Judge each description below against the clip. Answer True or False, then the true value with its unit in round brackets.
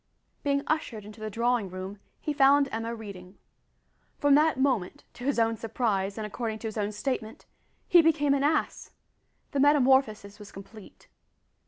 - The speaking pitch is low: False (230 Hz)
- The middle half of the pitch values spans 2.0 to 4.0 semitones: False (5.0 semitones)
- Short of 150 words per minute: False (160 wpm)